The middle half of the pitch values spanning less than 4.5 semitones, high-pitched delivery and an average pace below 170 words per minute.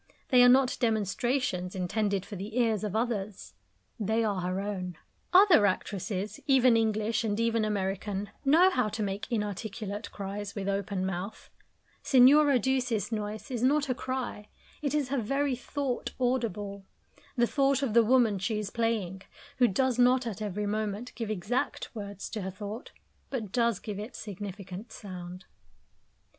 Yes: average, 3.7 semitones; high, 215 Hz; average, 155 wpm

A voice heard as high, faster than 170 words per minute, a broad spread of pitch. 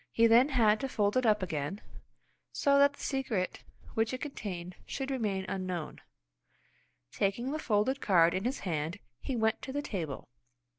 No: high, 215 Hz; average, 165 wpm; wide, 6.0 semitones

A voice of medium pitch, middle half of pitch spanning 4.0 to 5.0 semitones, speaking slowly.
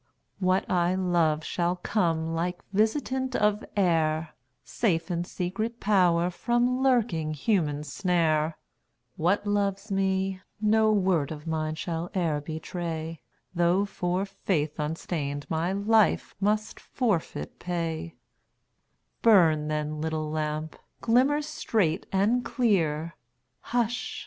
Yes: medium, 175 Hz; average, 4.4 semitones; slow, 110 wpm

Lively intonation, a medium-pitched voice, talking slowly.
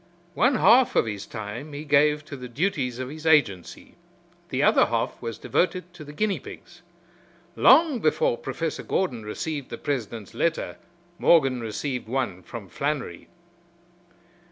No: wide, 6.7 semitones; medium, 145 Hz; average, 145 wpm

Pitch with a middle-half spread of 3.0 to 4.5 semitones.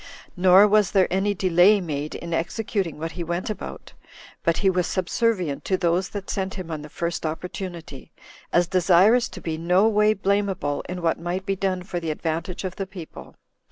No: narrow, 2.6 semitones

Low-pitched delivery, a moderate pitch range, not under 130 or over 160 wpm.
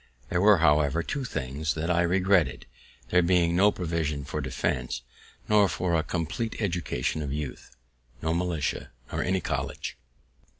Yes: very low, 85 Hz; average, 3.2 semitones; average, 145 wpm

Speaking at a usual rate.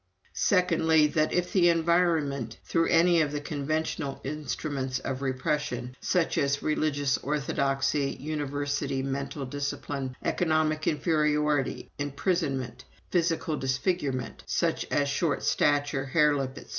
No: slow, 115 wpm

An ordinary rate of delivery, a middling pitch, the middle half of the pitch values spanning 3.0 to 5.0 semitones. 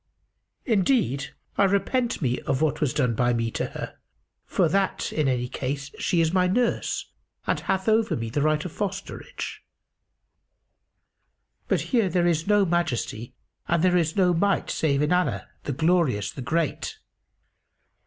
No: average, 155 wpm; medium, 165 Hz; wide, 5.5 semitones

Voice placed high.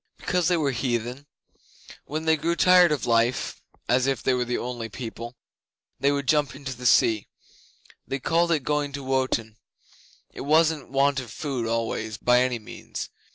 No: low, 130 Hz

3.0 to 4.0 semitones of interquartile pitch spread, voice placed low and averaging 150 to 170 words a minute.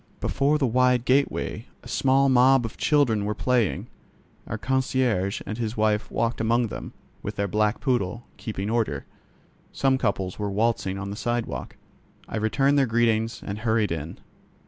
Yes: average, 3.4 semitones; low, 115 Hz; average, 160 wpm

